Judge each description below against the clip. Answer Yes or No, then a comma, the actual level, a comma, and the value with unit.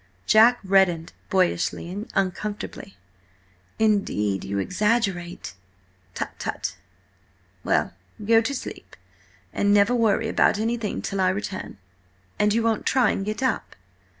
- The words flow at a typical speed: No, slow, 125 wpm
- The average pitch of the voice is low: No, high, 205 Hz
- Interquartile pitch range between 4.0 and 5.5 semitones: No, average, 3.2 semitones